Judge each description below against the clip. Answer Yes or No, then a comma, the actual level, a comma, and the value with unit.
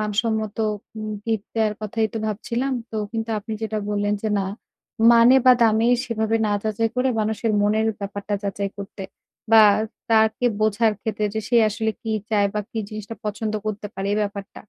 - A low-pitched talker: No, high, 215 Hz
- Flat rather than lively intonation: Yes, narrow, 1.4 semitones